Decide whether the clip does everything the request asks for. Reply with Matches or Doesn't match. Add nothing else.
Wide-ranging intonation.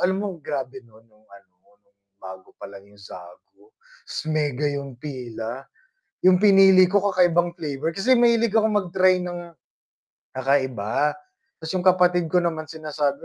Matches